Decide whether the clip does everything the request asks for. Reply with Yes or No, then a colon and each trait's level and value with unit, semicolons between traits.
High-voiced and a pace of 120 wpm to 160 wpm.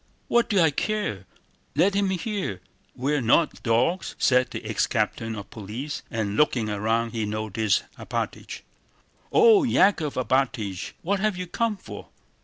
No: low, 130 Hz; average, 145 wpm